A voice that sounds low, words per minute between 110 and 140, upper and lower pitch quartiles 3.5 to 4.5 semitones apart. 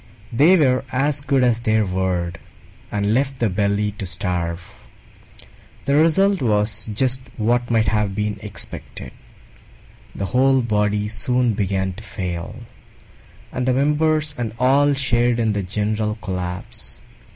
Yes: low, 110 Hz; slow, 135 wpm; average, 4.2 semitones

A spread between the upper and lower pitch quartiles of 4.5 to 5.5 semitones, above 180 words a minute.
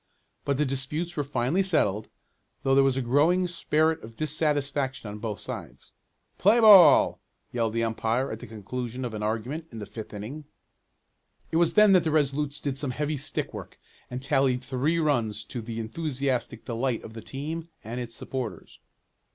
No: average, 4.9 semitones; average, 175 wpm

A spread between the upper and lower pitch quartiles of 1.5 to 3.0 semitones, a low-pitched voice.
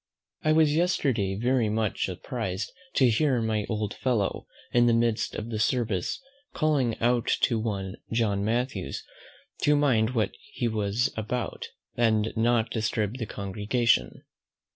Yes: average, 2.7 semitones; low, 115 Hz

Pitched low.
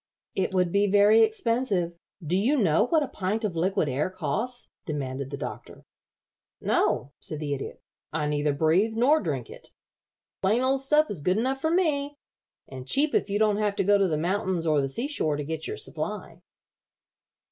No: high, 195 Hz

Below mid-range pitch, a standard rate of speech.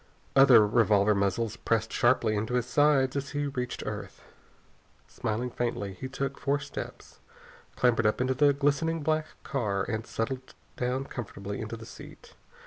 Yes: low, 125 Hz; average, 150 wpm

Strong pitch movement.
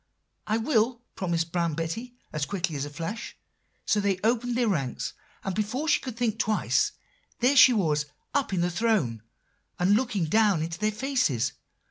Yes: wide, 5.9 semitones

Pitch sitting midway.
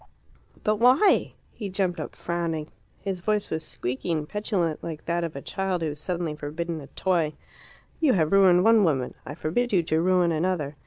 Yes: medium, 170 Hz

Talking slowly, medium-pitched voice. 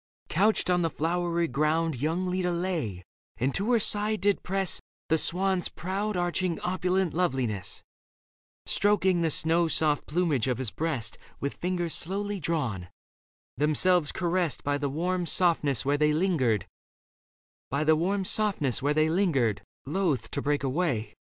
Yes: slow, 125 wpm; medium, 165 Hz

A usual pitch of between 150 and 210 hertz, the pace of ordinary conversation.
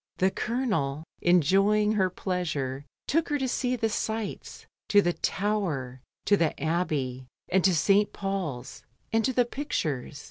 Yes: high, 190 Hz; average, 145 wpm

